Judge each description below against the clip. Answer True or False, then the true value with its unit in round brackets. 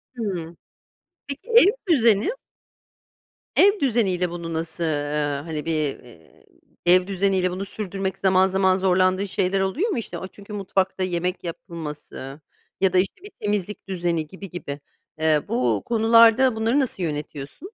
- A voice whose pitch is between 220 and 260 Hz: False (185 Hz)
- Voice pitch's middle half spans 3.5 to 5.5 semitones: True (3.8 semitones)